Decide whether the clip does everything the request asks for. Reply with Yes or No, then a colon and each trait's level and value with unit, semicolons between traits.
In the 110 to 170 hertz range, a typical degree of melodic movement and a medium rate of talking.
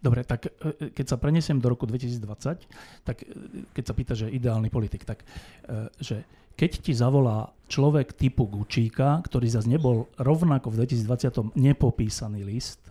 Yes: low, 125 Hz; average, 3.4 semitones; average, 145 wpm